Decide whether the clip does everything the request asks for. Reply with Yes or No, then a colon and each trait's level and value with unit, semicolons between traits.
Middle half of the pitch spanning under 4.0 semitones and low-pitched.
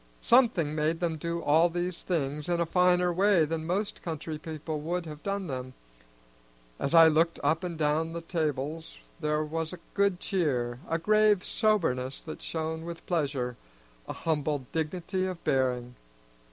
No: average, 2.8 semitones; medium, 165 Hz